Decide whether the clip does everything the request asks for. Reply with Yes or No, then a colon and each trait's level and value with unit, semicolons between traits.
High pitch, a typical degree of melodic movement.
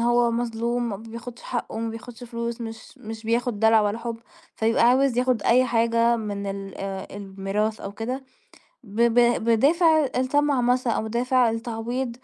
No: high, 235 Hz; narrow, 1.8 semitones